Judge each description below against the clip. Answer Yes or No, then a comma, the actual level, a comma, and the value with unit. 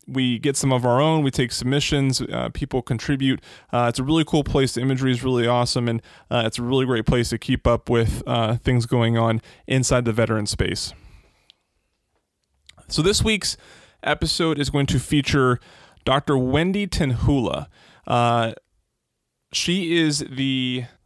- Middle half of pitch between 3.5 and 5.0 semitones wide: No, average, 2.9 semitones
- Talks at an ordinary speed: Yes, average, 160 wpm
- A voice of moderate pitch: No, low, 130 Hz